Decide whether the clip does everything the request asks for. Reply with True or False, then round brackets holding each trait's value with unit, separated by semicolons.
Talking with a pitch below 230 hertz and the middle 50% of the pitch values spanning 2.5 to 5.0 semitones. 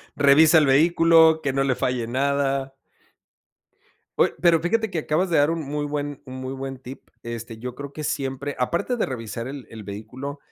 True (140 Hz; 3.3 semitones)